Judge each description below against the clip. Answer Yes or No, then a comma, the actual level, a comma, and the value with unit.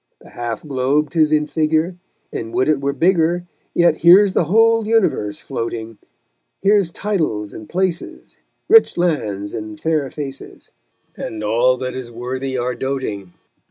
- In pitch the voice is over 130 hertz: Yes, medium, 140 Hz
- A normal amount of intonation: No, wide, 6.4 semitones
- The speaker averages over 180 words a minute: No, average, 145 wpm